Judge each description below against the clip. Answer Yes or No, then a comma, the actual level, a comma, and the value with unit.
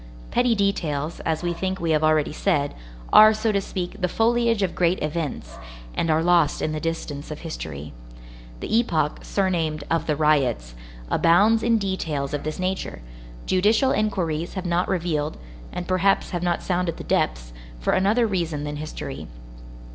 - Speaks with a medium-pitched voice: Yes, medium, 170 Hz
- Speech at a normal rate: Yes, average, 165 wpm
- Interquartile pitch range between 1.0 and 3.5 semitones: No, average, 4.2 semitones